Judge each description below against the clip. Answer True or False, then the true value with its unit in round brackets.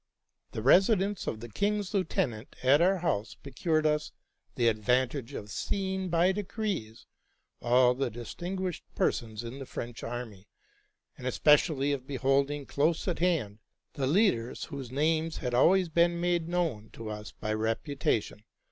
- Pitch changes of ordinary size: False (6.6 semitones)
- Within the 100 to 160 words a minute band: True (150 wpm)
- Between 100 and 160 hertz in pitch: True (140 Hz)